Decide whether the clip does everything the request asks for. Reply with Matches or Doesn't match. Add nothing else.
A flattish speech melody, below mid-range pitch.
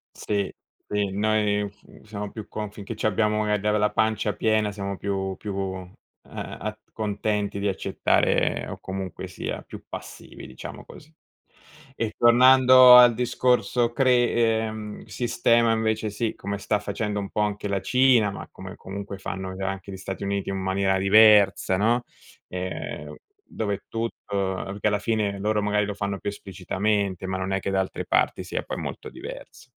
Matches